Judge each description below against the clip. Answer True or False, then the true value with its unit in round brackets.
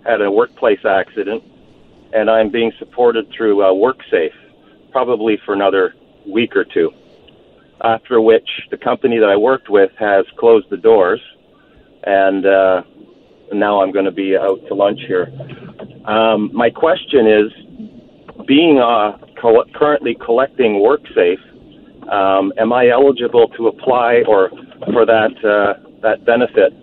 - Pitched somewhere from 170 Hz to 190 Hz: False (120 Hz)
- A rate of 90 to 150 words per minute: True (140 wpm)